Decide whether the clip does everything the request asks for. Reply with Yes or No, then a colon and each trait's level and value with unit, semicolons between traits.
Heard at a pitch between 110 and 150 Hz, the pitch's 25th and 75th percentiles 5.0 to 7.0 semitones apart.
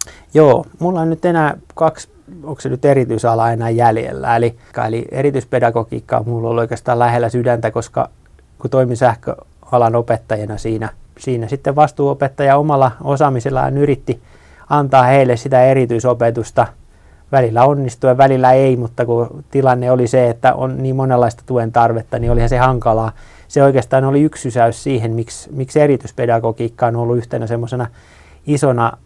No: low, 125 Hz; narrow, 2.6 semitones